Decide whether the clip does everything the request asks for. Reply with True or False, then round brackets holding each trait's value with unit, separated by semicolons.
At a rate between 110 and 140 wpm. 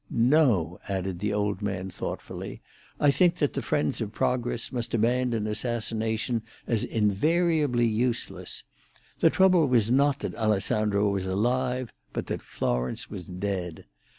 True (135 wpm)